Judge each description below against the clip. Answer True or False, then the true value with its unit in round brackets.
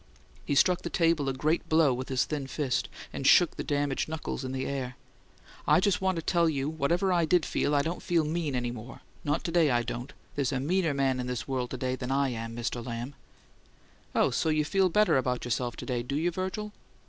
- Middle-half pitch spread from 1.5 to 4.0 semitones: False (4.5 semitones)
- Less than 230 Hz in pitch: True (140 Hz)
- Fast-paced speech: True (225 wpm)